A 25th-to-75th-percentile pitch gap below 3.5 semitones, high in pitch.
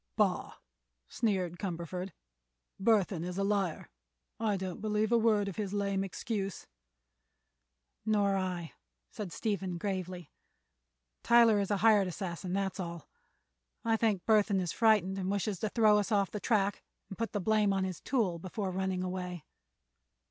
Yes: narrow, 2.4 semitones; high, 195 Hz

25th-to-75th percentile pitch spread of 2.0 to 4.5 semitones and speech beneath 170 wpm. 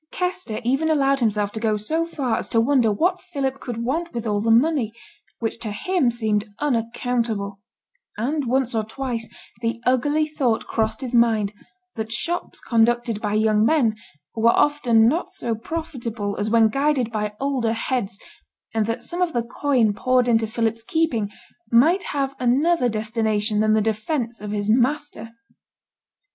Yes: average, 3.9 semitones; average, 160 wpm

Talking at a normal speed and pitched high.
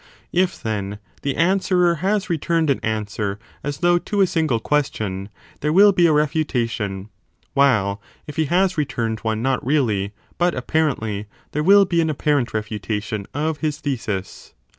No: average, 160 wpm; medium, 140 Hz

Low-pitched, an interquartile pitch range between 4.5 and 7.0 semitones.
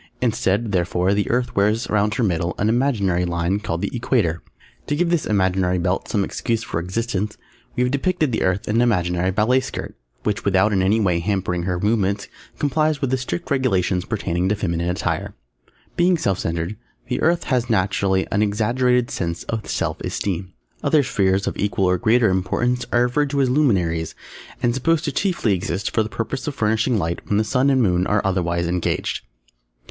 Yes: low, 105 Hz; average, 5.1 semitones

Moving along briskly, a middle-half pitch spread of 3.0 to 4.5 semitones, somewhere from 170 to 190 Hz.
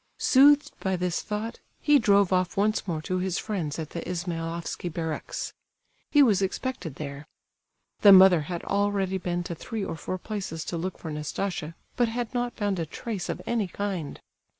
No: average, 175 wpm; average, 3.7 semitones; medium, 185 Hz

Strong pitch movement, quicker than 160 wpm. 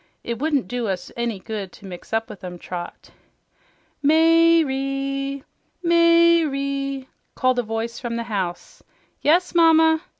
No: wide, 6.1 semitones; average, 140 wpm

